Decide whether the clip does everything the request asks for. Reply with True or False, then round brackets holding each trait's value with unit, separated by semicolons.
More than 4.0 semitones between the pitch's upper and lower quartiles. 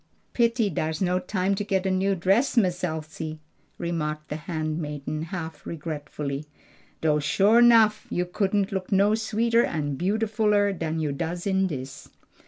True (4.6 semitones)